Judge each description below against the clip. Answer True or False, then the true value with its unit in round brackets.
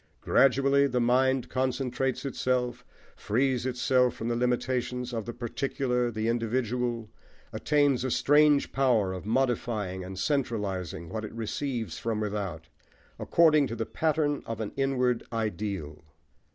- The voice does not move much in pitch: False (3.2 semitones)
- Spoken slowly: True (130 wpm)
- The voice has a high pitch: False (125 Hz)